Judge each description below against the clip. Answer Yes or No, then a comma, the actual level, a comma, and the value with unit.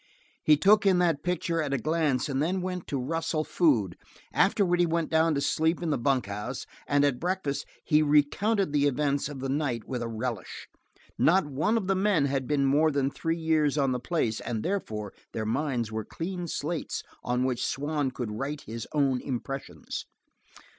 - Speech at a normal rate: Yes, average, 190 wpm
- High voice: No, medium, 145 Hz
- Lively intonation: No, average, 4.3 semitones